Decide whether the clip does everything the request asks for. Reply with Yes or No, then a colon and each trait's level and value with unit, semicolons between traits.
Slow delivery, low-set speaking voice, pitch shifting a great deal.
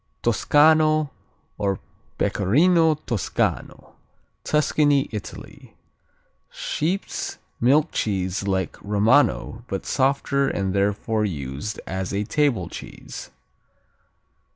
Yes: slow, 80 wpm; low, 110 Hz; wide, 7.3 semitones